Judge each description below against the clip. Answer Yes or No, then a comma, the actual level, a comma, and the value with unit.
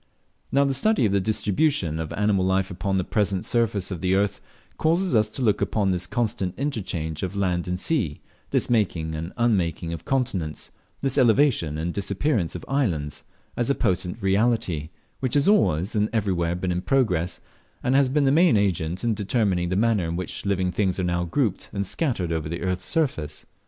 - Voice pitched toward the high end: No, low, 100 Hz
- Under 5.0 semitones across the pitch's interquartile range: No, wide, 5.4 semitones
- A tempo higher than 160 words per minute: Yes, average, 190 wpm